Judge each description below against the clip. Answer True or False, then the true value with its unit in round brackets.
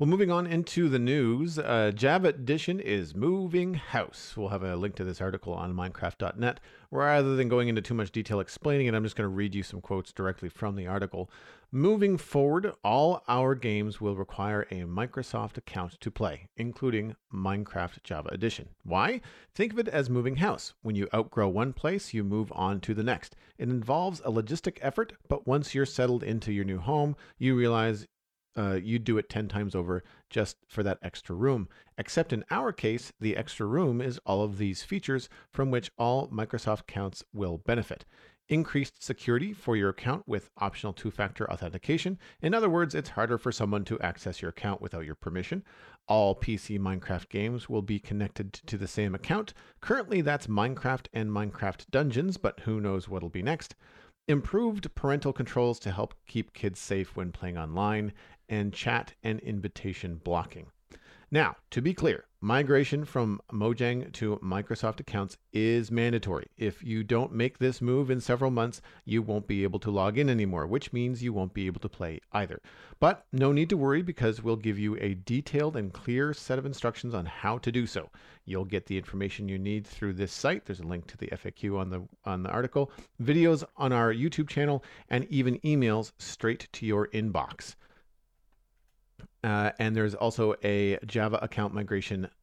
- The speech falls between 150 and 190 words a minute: True (185 wpm)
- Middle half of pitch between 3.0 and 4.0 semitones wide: False (4.8 semitones)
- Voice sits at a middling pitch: False (110 Hz)